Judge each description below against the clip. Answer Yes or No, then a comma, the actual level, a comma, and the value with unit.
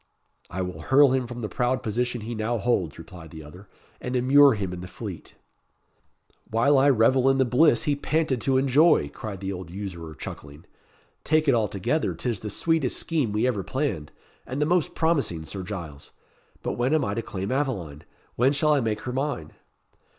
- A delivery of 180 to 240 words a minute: Yes, average, 190 wpm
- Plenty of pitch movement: Yes, wide, 6.3 semitones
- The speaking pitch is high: No, low, 120 Hz